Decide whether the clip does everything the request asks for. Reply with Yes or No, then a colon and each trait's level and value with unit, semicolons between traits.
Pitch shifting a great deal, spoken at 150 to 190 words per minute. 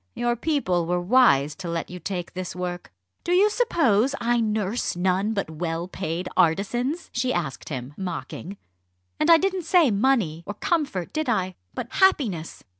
Yes: wide, 7.0 semitones; average, 165 wpm